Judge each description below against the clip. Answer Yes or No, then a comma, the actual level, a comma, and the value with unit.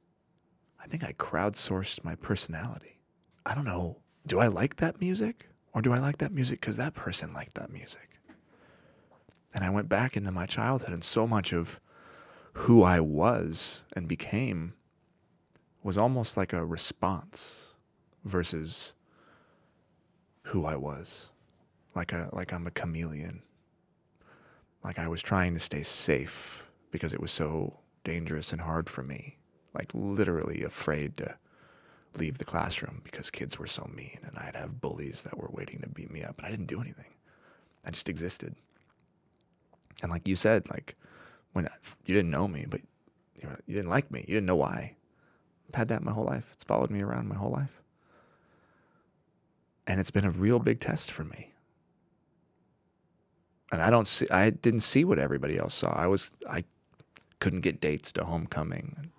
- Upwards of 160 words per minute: Yes, average, 170 wpm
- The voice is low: Yes, very low, 95 Hz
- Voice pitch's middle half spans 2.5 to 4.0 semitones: No, wide, 5.6 semitones